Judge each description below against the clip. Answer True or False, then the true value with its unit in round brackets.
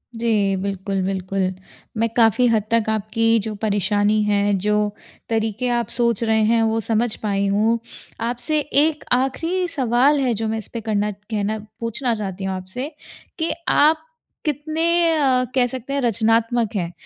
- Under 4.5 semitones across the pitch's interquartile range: True (3.2 semitones)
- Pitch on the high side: True (225 Hz)